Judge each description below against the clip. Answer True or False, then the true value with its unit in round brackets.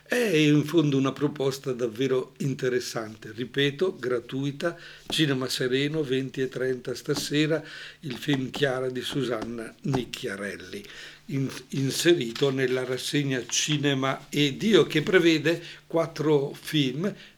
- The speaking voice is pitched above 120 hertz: True (140 Hz)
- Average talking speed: False (100 wpm)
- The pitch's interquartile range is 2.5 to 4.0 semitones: True (3.2 semitones)